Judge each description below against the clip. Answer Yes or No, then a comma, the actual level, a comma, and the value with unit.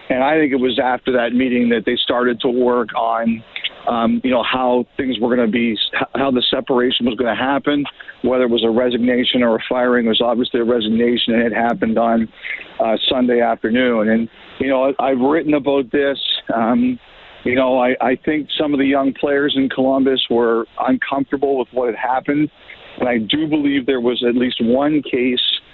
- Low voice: Yes, low, 125 Hz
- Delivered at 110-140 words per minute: No, average, 200 wpm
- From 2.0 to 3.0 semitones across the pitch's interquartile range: Yes, narrow, 2.4 semitones